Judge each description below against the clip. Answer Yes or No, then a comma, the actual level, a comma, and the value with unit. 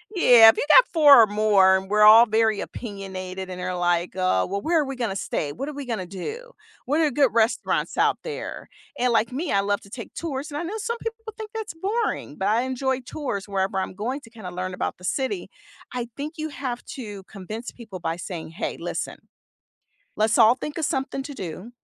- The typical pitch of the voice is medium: No, high, 230 Hz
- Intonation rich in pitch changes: Yes, wide, 6.6 semitones